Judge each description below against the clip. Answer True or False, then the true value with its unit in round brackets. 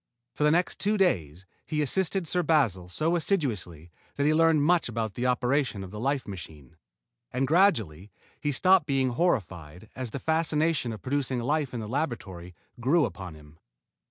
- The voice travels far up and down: True (8.4 semitones)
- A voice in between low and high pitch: False (130 Hz)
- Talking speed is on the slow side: False (170 wpm)